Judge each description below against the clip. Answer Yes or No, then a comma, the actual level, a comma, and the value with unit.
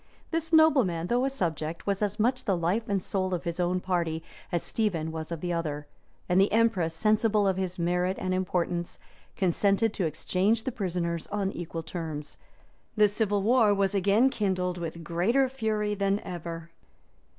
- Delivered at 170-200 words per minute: Yes, average, 175 wpm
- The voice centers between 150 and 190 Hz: Yes, medium, 185 Hz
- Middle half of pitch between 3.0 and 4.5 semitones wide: Yes, average, 3.8 semitones